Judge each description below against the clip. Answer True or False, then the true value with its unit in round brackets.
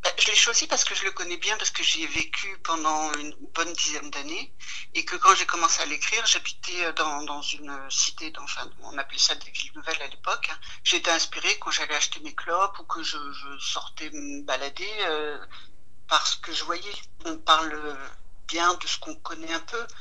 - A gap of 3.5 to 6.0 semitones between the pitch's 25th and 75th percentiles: False (2.8 semitones)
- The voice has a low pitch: False (155 Hz)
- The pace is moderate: True (205 wpm)